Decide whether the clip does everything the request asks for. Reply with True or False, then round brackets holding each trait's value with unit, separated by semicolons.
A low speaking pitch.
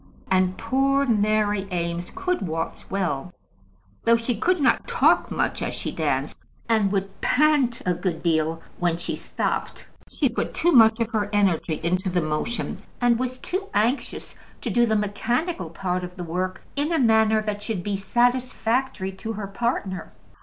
False (210 Hz)